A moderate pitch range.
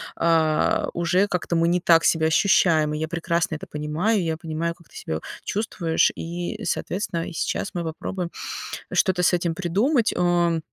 No: narrow, 1.7 semitones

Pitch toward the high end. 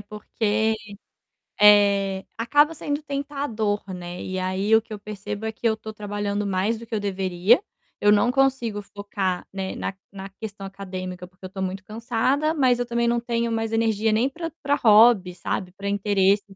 Yes: high, 210 Hz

